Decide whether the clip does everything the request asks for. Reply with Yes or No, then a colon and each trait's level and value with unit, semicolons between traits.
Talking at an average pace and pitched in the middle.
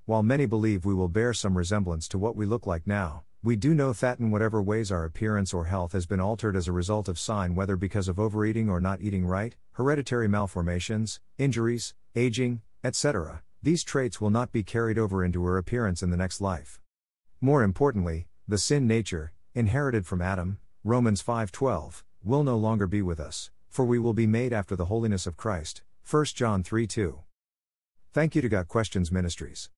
No: average, 195 wpm; low, 105 Hz